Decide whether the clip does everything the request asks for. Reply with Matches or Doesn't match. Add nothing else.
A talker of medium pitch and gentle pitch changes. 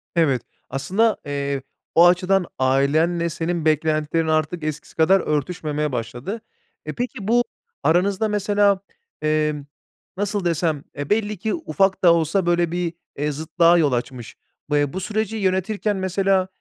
Doesn't match